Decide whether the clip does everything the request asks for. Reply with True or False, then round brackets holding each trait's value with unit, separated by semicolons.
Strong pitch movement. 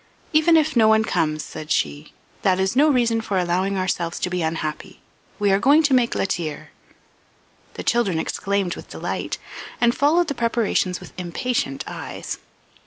True (6.0 semitones)